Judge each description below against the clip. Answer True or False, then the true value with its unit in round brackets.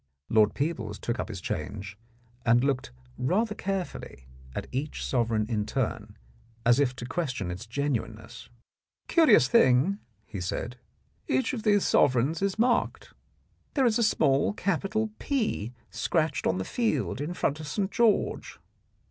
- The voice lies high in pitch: False (140 Hz)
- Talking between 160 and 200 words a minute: False (150 wpm)